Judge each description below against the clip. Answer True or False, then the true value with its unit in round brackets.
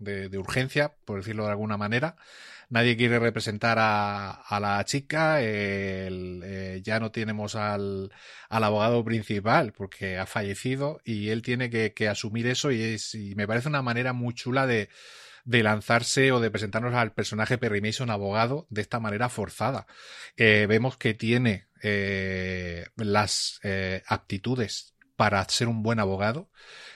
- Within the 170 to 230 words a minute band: False (160 wpm)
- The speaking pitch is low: True (110 Hz)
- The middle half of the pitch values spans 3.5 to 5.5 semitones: False (2.9 semitones)